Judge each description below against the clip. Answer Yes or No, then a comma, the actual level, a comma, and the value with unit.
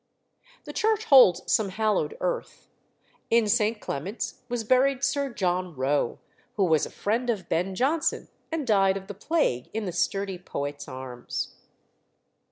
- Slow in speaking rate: No, average, 150 wpm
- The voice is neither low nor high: No, high, 200 Hz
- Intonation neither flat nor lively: No, wide, 5.7 semitones